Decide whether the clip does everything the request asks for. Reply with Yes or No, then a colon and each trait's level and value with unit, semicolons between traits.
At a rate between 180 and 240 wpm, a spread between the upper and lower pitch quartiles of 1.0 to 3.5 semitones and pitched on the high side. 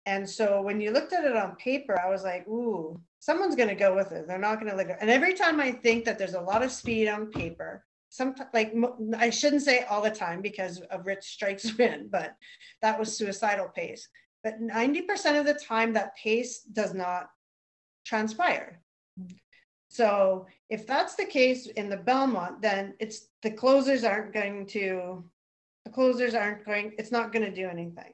No: average, 195 wpm; average, 4.1 semitones; high, 220 Hz